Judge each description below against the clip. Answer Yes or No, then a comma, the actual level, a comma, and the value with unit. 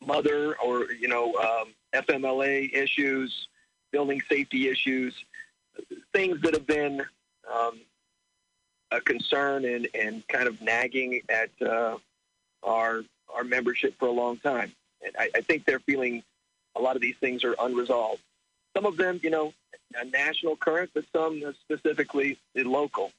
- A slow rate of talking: No, average, 145 wpm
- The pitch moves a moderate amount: Yes, average, 3.8 semitones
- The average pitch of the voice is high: No, low, 135 Hz